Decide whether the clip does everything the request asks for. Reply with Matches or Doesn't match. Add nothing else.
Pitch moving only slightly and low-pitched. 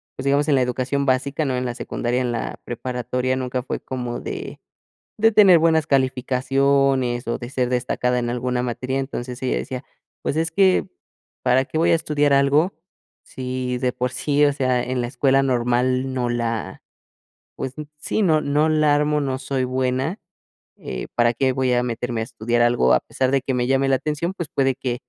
Matches